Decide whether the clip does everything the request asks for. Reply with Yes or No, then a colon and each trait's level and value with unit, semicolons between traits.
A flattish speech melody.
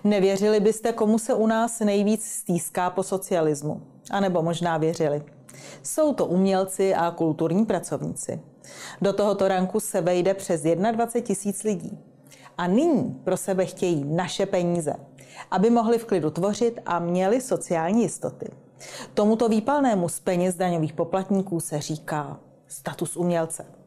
No: average, 4.0 semitones